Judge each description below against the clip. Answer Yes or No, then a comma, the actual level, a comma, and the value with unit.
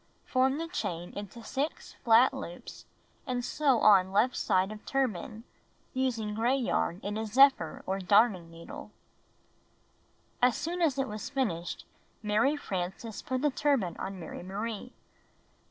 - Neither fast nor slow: Yes, average, 145 wpm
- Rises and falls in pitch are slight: No, wide, 5.4 semitones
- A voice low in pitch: No, high, 225 Hz